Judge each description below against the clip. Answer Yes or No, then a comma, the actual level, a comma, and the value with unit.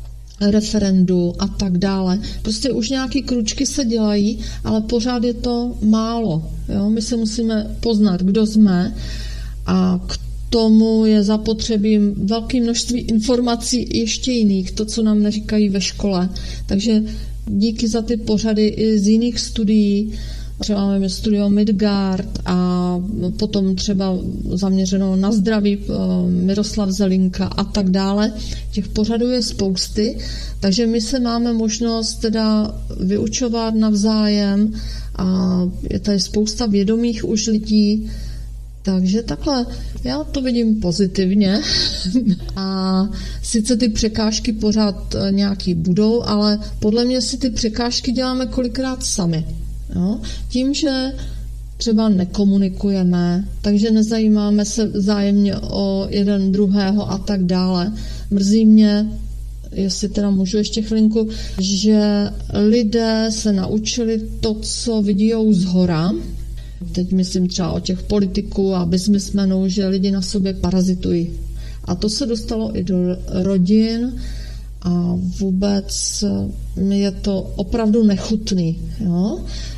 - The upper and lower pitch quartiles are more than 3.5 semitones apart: No, average, 2.8 semitones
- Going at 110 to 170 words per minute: Yes, average, 120 wpm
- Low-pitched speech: No, high, 205 Hz